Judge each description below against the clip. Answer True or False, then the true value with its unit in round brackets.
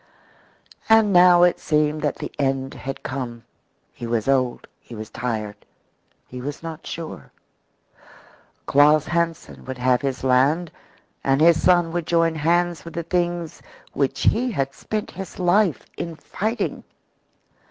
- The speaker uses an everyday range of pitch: True (4.6 semitones)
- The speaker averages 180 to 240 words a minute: False (140 wpm)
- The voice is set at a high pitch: False (155 Hz)